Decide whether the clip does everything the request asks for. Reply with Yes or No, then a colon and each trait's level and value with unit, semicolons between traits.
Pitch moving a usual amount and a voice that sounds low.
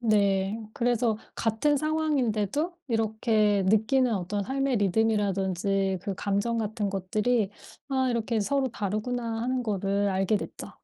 No: average, 3.5 semitones; high, 220 Hz